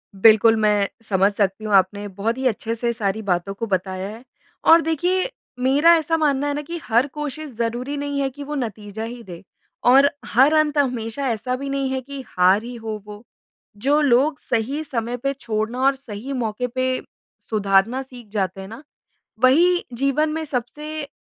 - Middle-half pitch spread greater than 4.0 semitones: Yes, average, 4.9 semitones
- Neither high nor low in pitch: No, high, 245 Hz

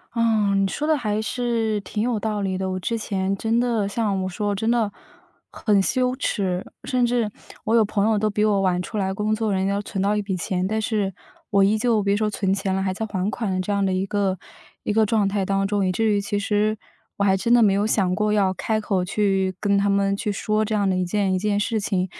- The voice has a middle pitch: No, high, 205 Hz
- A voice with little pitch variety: Yes, narrow, 2.0 semitones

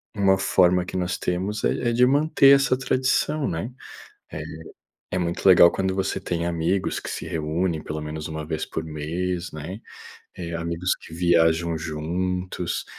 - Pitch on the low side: Yes, very low, 90 Hz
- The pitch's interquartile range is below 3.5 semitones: Yes, average, 2.7 semitones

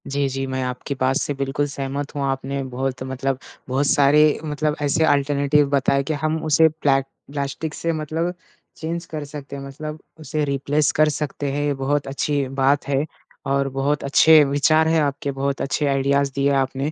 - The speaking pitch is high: No, medium, 140 Hz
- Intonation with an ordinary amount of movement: No, narrow, 1.6 semitones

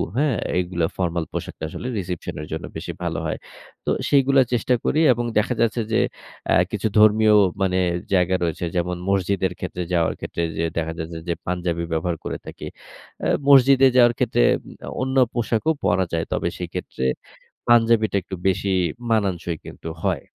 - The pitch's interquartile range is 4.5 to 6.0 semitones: Yes, average, 5.1 semitones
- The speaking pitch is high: No, very low, 95 Hz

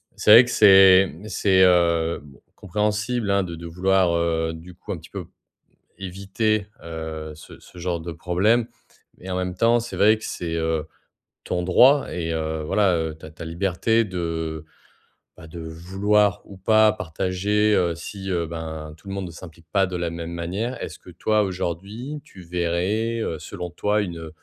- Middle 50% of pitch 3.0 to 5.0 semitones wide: Yes, average, 3.7 semitones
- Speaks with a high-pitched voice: No, very low, 90 Hz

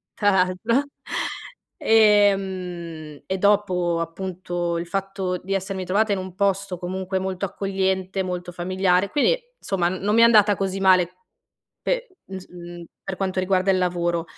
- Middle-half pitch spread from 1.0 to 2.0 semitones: Yes, narrow, 1.7 semitones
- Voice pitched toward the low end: No, high, 190 Hz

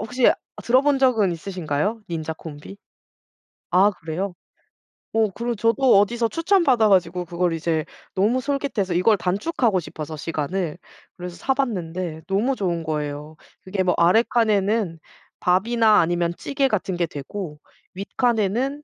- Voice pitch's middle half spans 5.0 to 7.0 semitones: Yes, wide, 5.4 semitones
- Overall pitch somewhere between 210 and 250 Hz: No, high, 195 Hz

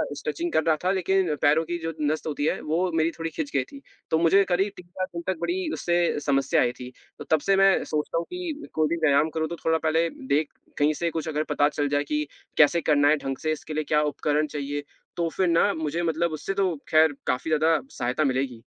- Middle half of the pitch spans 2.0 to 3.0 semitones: Yes, narrow, 2.6 semitones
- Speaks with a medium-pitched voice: Yes, medium, 160 Hz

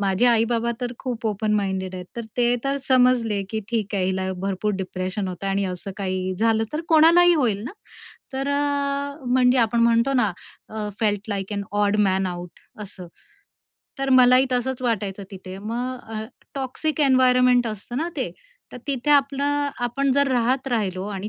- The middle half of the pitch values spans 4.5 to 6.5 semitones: Yes, average, 4.8 semitones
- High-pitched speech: Yes, high, 235 Hz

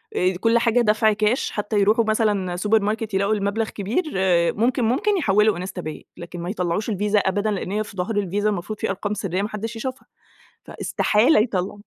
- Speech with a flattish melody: Yes, narrow, 2.3 semitones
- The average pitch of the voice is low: No, high, 210 Hz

